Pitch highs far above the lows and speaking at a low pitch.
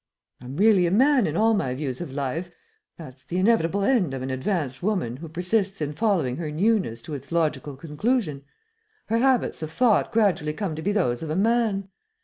No: wide, 6.5 semitones; medium, 170 Hz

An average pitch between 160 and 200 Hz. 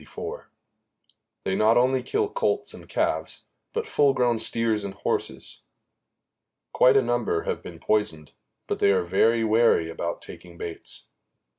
No: low, 115 Hz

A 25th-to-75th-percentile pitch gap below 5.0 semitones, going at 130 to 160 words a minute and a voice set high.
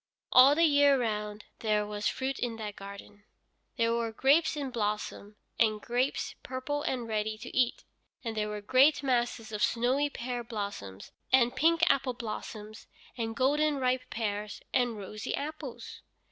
Yes: average, 3.9 semitones; average, 155 wpm; high, 235 Hz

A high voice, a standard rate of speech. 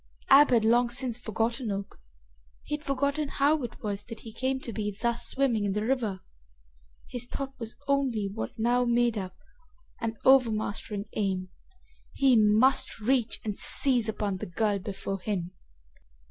Yes: high, 230 Hz; average, 160 wpm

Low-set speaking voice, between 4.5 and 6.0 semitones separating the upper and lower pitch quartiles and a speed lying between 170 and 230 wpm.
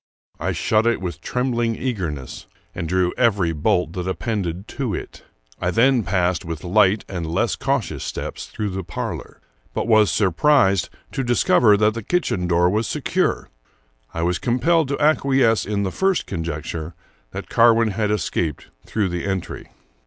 No: low, 100 Hz; average, 4.9 semitones; average, 160 wpm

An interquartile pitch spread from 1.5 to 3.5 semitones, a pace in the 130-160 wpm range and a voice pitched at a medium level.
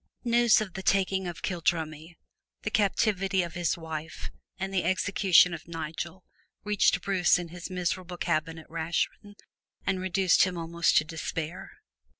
Yes: narrow, 2.6 semitones; average, 150 wpm; medium, 175 Hz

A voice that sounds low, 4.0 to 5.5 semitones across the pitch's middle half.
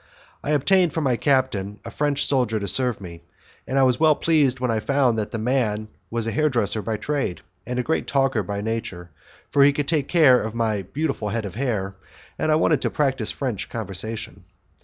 Yes: low, 125 Hz; average, 4.6 semitones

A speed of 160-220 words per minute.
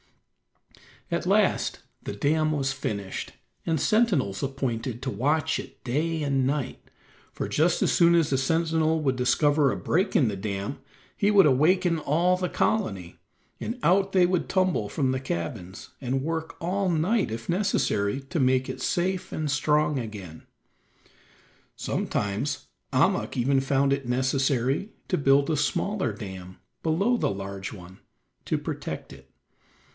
No: average, 150 wpm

